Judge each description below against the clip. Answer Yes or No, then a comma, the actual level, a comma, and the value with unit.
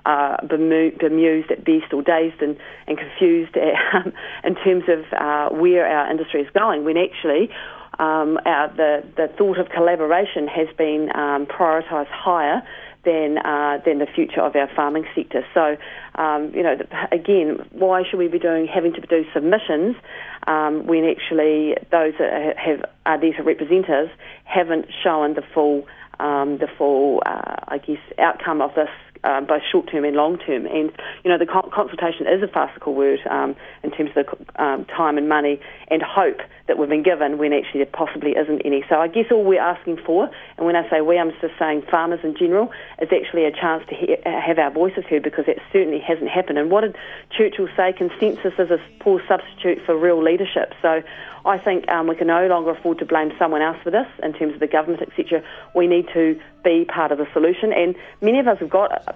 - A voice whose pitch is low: No, medium, 165 Hz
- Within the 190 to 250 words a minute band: Yes, average, 195 wpm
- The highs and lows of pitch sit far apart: No, narrow, 2.5 semitones